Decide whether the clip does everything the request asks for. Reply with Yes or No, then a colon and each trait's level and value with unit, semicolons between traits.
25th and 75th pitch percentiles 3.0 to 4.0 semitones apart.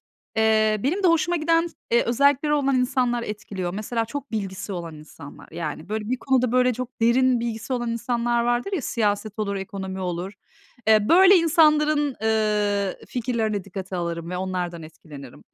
No: average, 4.9 semitones